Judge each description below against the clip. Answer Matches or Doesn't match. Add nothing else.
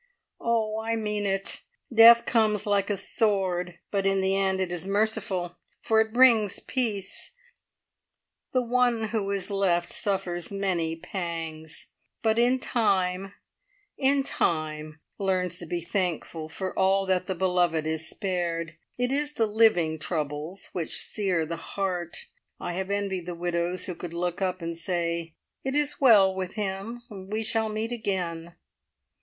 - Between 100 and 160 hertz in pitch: Doesn't match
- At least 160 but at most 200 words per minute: Doesn't match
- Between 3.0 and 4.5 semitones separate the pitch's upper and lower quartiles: Matches